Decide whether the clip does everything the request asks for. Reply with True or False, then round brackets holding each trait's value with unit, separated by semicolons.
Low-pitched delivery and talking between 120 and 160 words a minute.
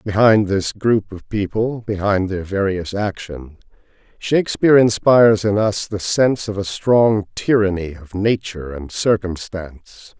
True (100 Hz; 135 wpm)